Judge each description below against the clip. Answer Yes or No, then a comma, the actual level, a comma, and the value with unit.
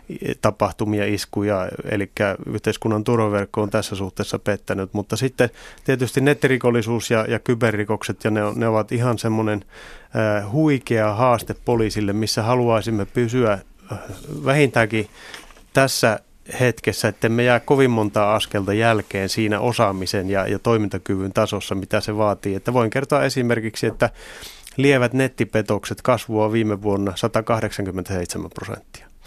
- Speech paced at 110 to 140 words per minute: Yes, average, 120 wpm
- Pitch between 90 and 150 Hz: Yes, low, 110 Hz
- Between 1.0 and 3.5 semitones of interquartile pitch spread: Yes, average, 2.7 semitones